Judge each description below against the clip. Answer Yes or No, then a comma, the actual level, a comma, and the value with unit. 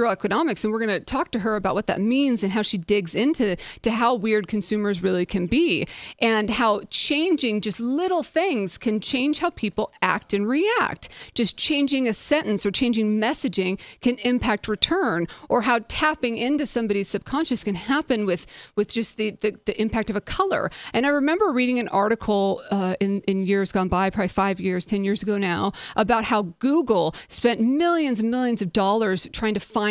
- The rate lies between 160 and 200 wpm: Yes, average, 195 wpm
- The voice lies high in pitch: Yes, high, 220 Hz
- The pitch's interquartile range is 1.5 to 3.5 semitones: No, average, 3.9 semitones